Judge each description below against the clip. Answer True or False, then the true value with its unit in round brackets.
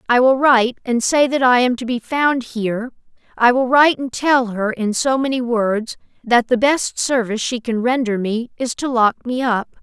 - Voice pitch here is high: True (245 Hz)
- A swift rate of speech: True (215 wpm)